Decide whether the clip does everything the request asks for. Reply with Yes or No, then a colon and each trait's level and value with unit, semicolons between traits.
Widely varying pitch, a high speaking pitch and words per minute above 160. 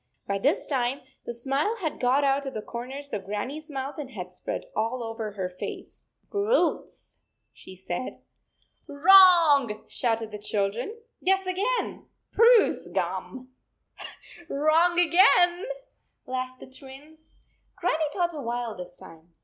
No: wide, 7.2 semitones; very high, 270 Hz; average, 150 wpm